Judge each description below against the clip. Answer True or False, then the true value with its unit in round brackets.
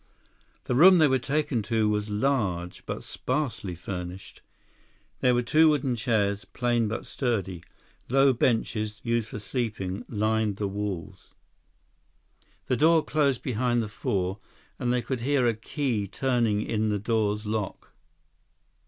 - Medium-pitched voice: False (115 Hz)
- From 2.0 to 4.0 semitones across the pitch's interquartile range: True (3.7 semitones)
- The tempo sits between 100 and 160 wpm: True (140 wpm)